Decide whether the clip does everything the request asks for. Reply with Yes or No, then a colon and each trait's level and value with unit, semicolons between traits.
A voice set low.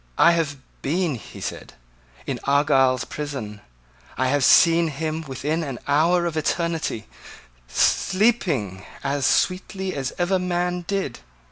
No: medium, 155 Hz